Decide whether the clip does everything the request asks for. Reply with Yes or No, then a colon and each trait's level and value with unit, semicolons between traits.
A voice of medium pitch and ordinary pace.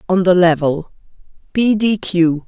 No: medium, 180 Hz; slow, 120 wpm